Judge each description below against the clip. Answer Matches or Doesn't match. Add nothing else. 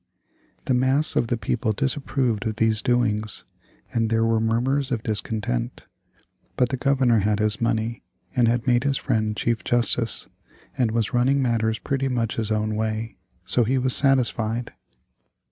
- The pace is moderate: Matches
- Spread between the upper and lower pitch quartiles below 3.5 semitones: Matches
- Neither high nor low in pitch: Doesn't match